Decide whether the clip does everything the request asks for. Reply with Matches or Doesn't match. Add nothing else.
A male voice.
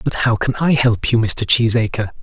Matches